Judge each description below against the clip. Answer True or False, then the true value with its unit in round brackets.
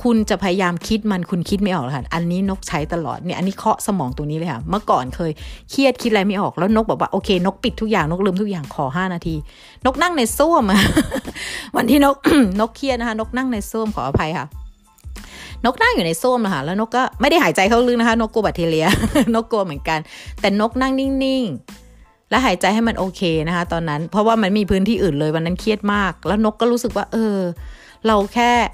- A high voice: True (205 Hz)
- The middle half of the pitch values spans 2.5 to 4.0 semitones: False (4.9 semitones)